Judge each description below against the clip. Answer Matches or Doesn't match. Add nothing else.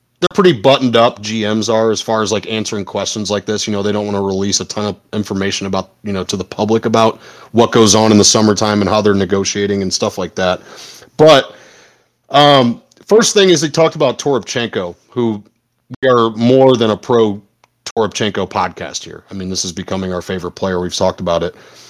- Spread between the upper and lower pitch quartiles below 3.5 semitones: Matches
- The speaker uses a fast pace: Matches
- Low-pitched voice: Matches